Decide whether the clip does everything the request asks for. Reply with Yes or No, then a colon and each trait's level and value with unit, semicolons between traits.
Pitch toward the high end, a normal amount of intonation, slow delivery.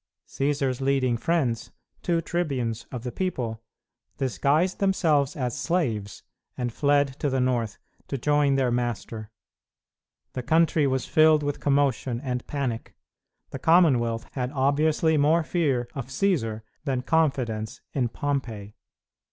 No: low, 135 Hz; average, 3.8 semitones; slow, 125 wpm